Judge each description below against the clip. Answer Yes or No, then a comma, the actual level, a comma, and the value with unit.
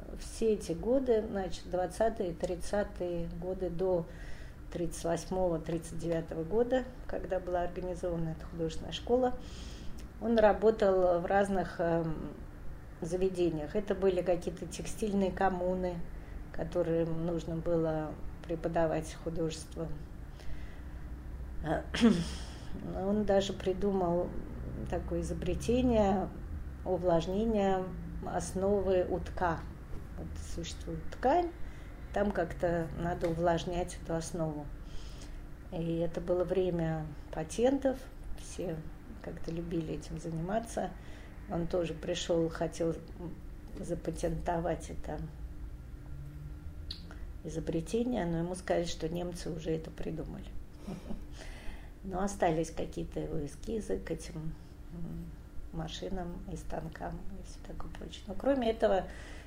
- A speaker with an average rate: No, slow, 90 wpm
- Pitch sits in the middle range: Yes, medium, 170 Hz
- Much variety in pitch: No, average, 2.9 semitones